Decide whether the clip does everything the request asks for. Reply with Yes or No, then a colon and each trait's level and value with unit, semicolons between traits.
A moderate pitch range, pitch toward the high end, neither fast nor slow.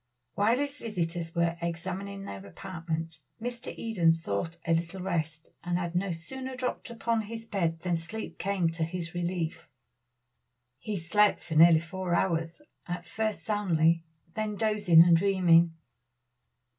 No: average, 3.9 semitones; medium, 175 Hz; average, 145 wpm